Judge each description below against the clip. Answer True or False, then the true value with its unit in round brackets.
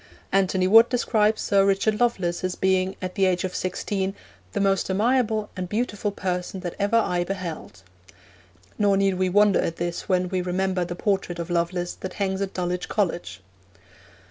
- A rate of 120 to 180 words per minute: True (170 wpm)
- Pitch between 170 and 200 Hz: True (190 Hz)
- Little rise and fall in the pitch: True (2.1 semitones)